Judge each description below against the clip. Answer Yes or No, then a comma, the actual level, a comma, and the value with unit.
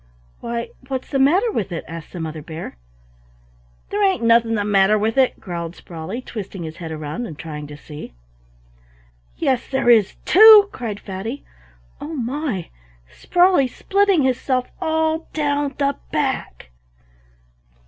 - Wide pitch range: Yes, wide, 8.6 semitones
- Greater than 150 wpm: No, average, 140 wpm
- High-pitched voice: Yes, high, 235 Hz